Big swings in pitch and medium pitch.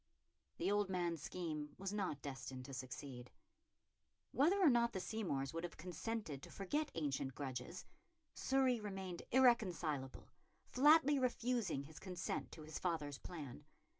Yes: wide, 7.9 semitones; medium, 175 Hz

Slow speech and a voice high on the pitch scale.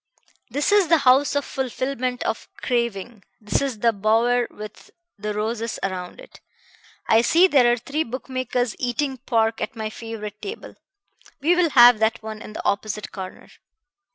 No: average, 160 wpm; high, 235 Hz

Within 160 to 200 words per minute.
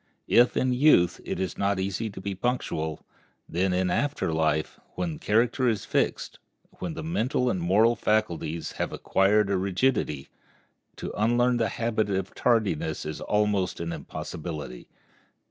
No: average, 150 wpm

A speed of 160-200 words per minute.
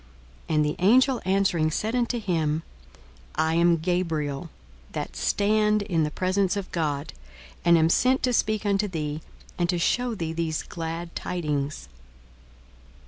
No: average, 145 wpm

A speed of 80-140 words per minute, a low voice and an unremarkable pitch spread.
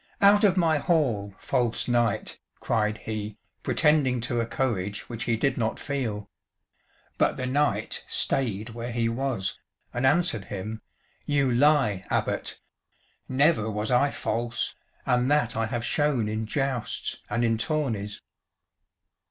Yes: slow, 135 wpm; low, 120 Hz; average, 4.1 semitones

